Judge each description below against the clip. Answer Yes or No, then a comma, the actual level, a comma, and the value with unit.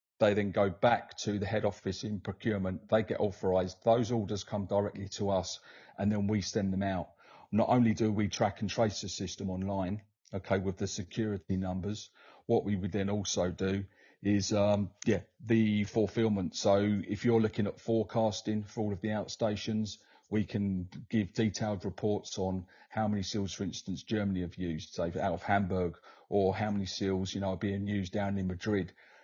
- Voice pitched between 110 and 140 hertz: No, low, 100 Hz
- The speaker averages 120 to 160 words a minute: No, average, 190 wpm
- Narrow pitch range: Yes, narrow, 1.8 semitones